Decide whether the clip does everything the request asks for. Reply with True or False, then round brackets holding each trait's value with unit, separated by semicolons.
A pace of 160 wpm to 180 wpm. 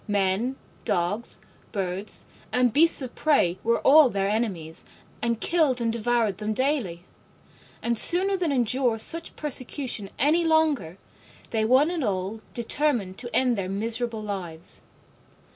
False (135 wpm)